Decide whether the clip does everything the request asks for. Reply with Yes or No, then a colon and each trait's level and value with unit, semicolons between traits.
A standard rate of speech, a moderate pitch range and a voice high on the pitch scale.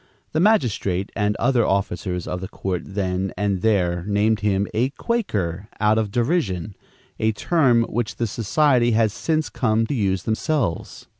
No: average, 155 wpm; average, 3.8 semitones; low, 110 Hz